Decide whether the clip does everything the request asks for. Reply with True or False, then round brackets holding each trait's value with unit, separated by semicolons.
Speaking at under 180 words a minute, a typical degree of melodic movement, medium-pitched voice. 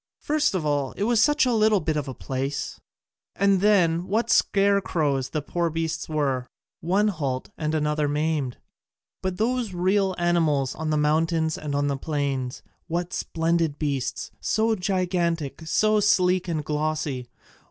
True (150 wpm; 4.3 semitones; 165 Hz)